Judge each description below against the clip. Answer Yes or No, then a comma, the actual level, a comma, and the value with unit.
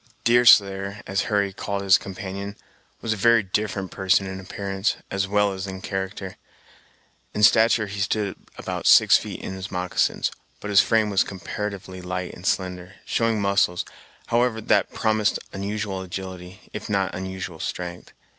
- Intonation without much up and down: Yes, narrow, 1.8 semitones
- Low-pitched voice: Yes, low, 100 Hz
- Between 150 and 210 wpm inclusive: Yes, average, 155 wpm